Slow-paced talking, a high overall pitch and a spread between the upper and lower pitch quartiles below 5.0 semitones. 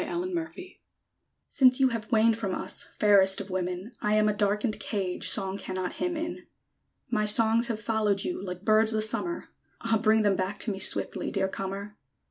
No: average, 190 wpm; high, 215 Hz; average, 2.7 semitones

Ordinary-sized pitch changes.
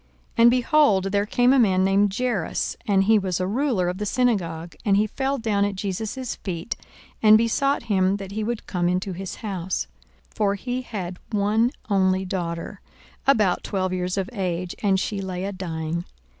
Yes: average, 3.2 semitones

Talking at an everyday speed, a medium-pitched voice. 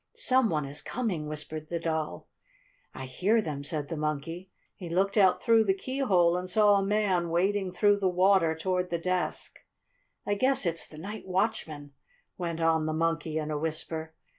Yes: average, 180 wpm; medium, 175 Hz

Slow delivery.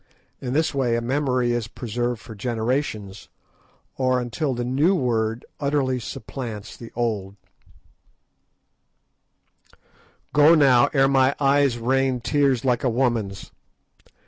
Yes: slow, 120 wpm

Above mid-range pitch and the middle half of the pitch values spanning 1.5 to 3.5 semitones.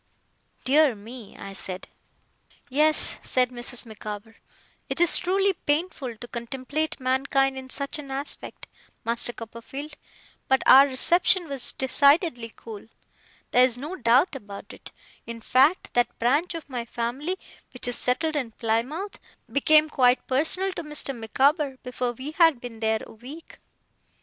No: very high, 260 Hz; average, 4.2 semitones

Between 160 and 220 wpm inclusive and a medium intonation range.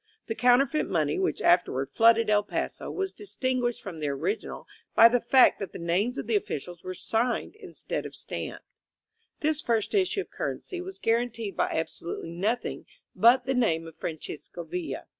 No: average, 175 wpm; wide, 6.6 semitones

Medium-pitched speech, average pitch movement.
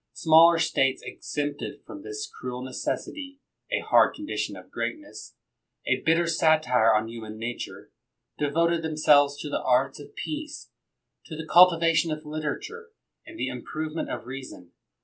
Yes: medium, 155 Hz; average, 4.1 semitones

